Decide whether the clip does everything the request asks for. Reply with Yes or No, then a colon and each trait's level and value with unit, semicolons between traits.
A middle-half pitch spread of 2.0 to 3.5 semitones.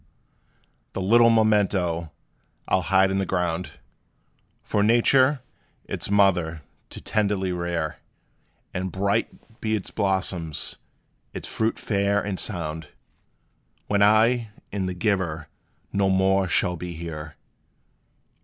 Yes: average, 2.9 semitones